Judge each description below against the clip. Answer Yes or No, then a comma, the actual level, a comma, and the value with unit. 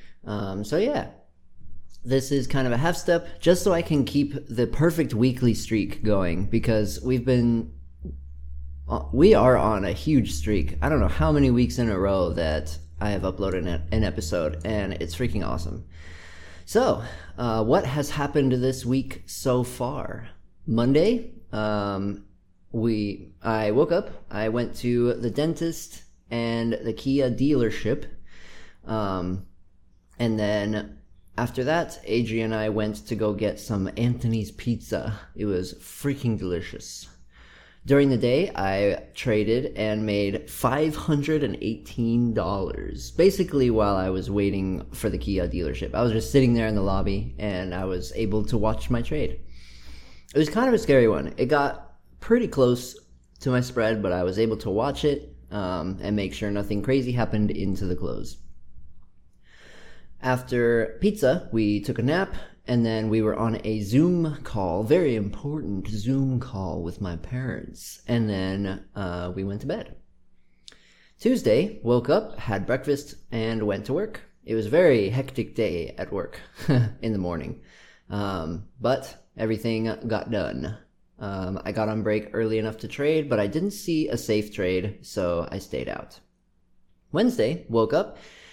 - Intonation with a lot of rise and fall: No, average, 4.7 semitones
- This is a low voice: Yes, low, 110 Hz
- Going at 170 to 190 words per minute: No, average, 160 wpm